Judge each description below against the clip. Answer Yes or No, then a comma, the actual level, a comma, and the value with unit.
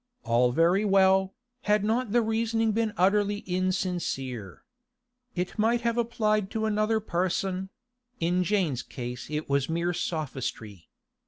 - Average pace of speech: No, slow, 130 wpm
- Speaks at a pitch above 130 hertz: Yes, high, 190 Hz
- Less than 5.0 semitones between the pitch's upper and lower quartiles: No, average, 5.3 semitones